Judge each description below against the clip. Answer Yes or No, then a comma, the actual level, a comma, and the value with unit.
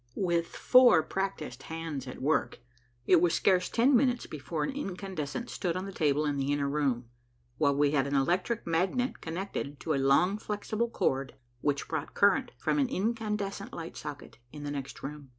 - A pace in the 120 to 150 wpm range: No, average, 180 wpm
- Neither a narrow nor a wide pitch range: No, wide, 5.9 semitones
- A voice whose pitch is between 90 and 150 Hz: No, medium, 165 Hz